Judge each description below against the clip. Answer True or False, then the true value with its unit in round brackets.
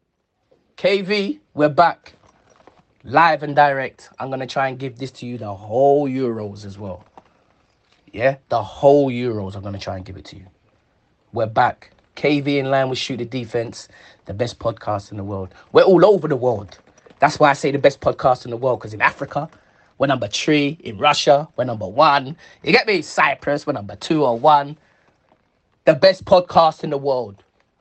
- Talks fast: False (190 wpm)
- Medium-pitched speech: False (130 Hz)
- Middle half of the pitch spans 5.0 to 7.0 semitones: True (5.4 semitones)